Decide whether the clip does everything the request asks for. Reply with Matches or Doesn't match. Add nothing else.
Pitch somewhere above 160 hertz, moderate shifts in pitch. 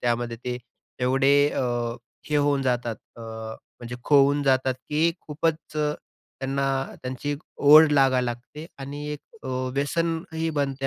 Doesn't match